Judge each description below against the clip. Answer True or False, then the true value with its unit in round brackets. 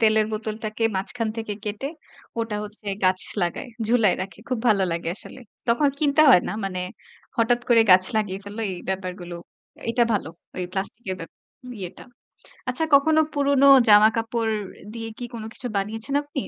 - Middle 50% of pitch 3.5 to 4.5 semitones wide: True (3.8 semitones)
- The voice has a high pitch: True (220 Hz)